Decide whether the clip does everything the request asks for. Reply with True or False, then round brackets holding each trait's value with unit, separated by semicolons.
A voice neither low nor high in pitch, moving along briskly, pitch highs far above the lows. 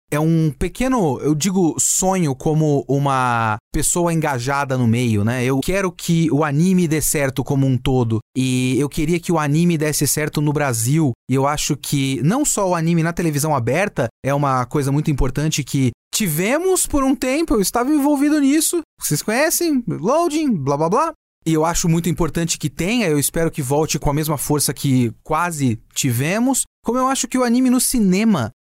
True (155 Hz; 190 wpm; 5.8 semitones)